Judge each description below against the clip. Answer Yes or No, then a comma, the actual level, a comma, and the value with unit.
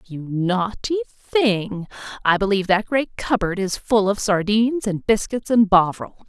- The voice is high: Yes, high, 205 Hz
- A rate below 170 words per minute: Yes, average, 155 wpm